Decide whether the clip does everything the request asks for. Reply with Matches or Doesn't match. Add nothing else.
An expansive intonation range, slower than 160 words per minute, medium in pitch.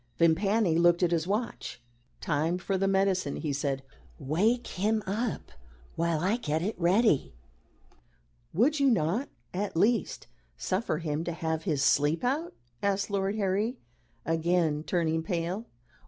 Doesn't match